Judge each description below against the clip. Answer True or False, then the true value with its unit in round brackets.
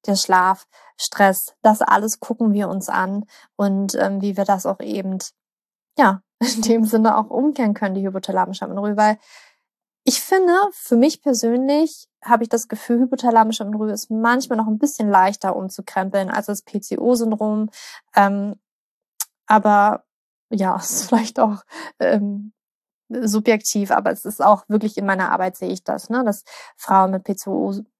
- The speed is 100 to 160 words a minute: True (155 wpm)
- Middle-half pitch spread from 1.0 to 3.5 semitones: True (2.9 semitones)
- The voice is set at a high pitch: True (215 Hz)